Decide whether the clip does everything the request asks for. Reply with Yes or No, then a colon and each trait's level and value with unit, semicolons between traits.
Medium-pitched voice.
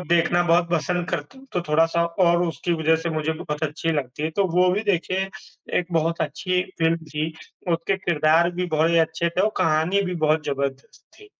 Yes: medium, 165 Hz